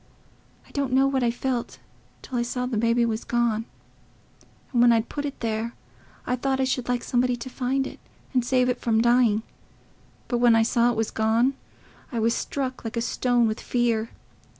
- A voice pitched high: Yes, high, 240 Hz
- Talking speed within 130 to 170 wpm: No, average, 195 wpm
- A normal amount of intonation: No, narrow, 1.6 semitones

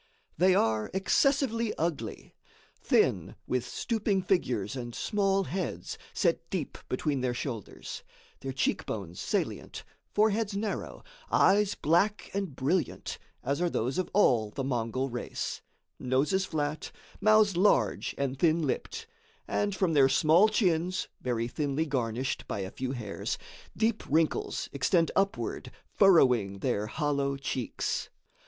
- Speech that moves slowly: Yes, slow, 130 wpm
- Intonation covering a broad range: Yes, wide, 7.3 semitones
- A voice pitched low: No, medium, 150 Hz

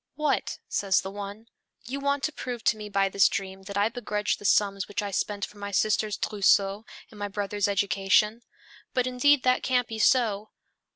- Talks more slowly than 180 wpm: No, average, 190 wpm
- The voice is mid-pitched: No, high, 210 Hz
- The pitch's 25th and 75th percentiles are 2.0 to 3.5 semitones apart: Yes, average, 3.2 semitones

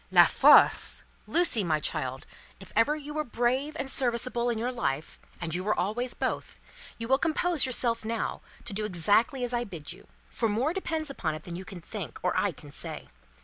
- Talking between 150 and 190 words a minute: No, average, 200 wpm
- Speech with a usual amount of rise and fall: No, wide, 5.9 semitones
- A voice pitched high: Yes, high, 235 Hz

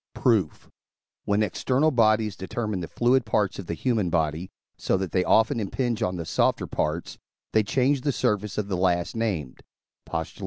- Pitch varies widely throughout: No, average, 4.5 semitones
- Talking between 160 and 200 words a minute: Yes, average, 170 wpm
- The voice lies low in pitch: Yes, low, 105 Hz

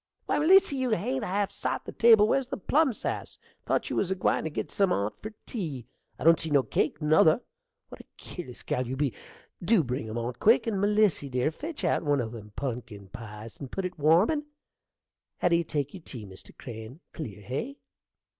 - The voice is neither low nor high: Yes, medium, 155 Hz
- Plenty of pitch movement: Yes, wide, 8.9 semitones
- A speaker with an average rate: No, fast, 210 wpm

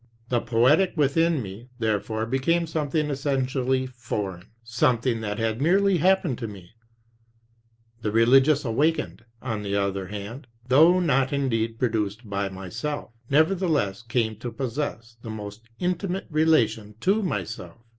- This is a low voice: Yes, low, 125 Hz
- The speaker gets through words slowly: Yes, slow, 130 wpm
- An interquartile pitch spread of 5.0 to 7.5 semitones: Yes, wide, 5.4 semitones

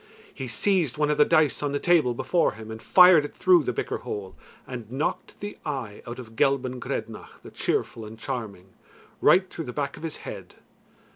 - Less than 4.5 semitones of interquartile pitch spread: No, wide, 5.5 semitones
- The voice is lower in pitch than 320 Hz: Yes, low, 135 Hz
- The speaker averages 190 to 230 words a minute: Yes, average, 200 wpm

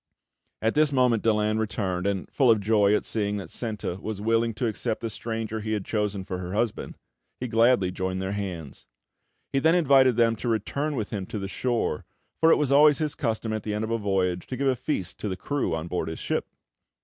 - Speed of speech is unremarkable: No, fast, 225 wpm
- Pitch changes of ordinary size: Yes, average, 3.7 semitones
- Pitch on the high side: No, low, 110 Hz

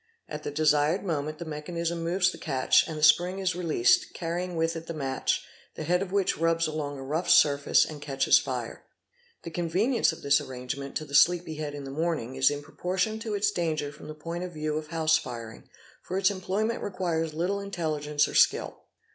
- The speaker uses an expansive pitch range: No, average, 3.2 semitones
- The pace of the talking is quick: Yes, fast, 210 wpm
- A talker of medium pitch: Yes, medium, 160 Hz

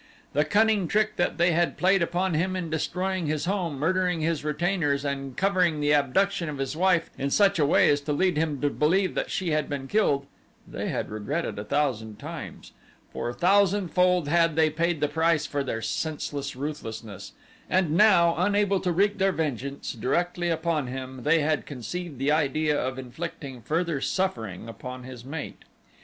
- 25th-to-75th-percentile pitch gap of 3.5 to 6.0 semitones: Yes, average, 4.4 semitones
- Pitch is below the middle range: No, medium, 155 Hz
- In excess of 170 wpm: Yes, average, 180 wpm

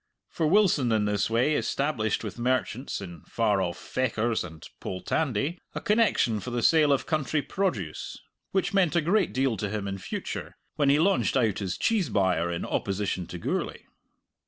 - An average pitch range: No, wide, 7.4 semitones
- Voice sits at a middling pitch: No, low, 120 Hz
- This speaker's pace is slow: No, average, 175 wpm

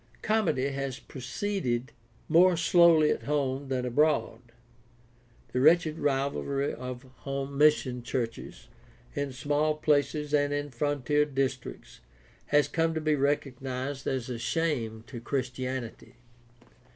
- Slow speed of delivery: Yes, slow, 115 wpm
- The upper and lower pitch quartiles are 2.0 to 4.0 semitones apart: Yes, average, 2.8 semitones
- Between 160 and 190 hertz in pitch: No, medium, 140 Hz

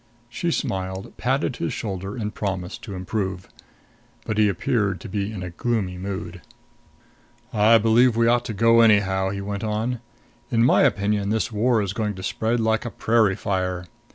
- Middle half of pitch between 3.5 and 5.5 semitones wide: No, average, 3.1 semitones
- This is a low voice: Yes, low, 105 Hz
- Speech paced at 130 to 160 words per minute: No, average, 175 wpm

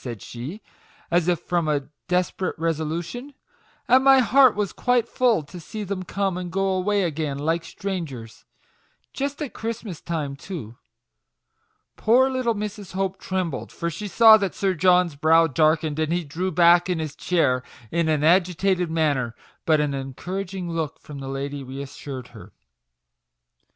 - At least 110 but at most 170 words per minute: Yes, average, 165 wpm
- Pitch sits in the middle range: Yes, medium, 175 Hz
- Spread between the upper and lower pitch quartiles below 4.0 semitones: No, average, 4.4 semitones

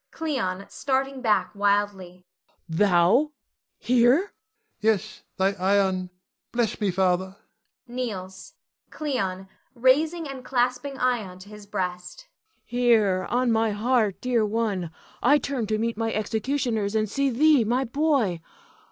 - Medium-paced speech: No, slow, 125 wpm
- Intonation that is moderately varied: Yes, average, 4.8 semitones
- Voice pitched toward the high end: Yes, high, 220 Hz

